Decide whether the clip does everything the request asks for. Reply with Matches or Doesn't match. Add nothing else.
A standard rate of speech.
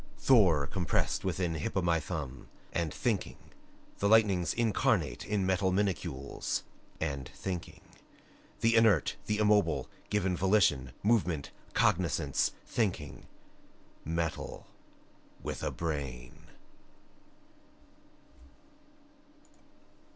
Doesn't match